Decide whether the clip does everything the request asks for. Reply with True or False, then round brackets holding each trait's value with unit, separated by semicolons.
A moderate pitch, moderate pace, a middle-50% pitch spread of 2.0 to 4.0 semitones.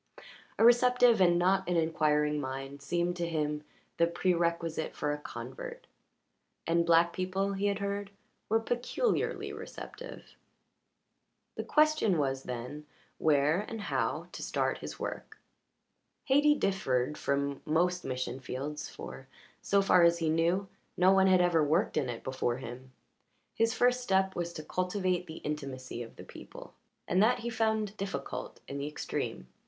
False (170 Hz; 150 wpm; 5.1 semitones)